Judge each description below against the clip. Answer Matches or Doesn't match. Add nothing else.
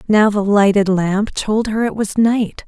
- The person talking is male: Doesn't match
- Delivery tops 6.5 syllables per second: Doesn't match